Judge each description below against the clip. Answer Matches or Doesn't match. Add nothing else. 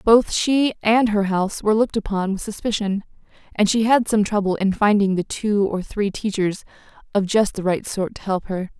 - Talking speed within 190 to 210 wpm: Matches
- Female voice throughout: Matches